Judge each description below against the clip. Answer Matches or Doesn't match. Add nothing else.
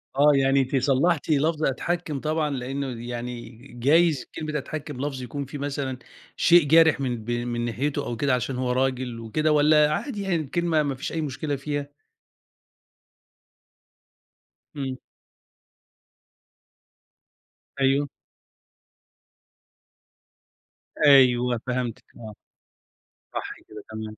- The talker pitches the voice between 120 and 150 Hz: Matches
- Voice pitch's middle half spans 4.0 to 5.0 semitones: Doesn't match